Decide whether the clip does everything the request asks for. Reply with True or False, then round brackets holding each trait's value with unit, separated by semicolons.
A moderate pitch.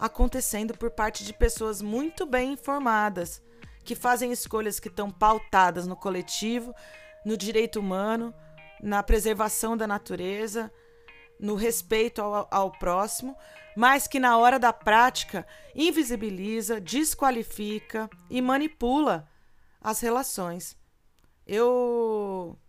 False (220 Hz)